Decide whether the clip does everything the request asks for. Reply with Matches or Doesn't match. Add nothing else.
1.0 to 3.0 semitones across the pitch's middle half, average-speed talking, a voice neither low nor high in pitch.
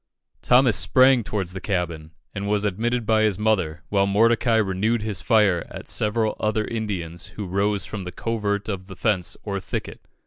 Doesn't match